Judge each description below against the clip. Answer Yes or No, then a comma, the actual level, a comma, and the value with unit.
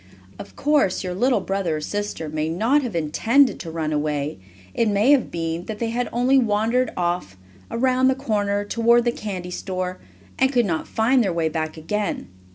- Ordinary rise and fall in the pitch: No, wide, 6.3 semitones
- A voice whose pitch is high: Yes, high, 205 Hz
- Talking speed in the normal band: Yes, average, 180 wpm